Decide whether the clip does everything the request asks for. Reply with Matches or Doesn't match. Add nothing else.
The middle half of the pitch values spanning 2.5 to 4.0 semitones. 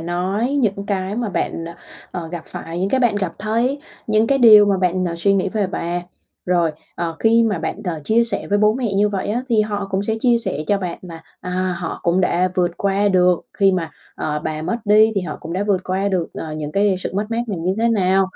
Matches